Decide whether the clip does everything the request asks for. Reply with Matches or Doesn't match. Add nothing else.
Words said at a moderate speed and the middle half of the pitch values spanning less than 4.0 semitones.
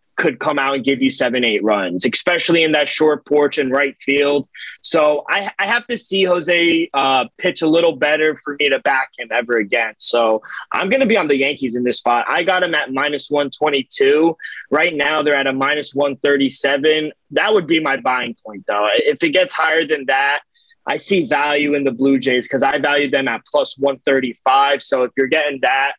Doesn't match